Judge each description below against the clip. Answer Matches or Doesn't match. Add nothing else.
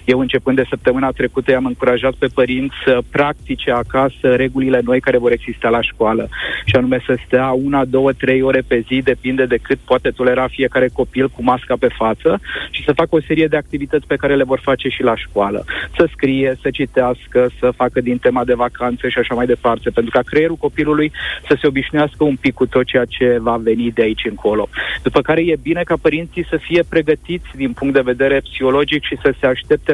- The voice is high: Doesn't match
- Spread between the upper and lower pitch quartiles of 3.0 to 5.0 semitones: Doesn't match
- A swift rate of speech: Matches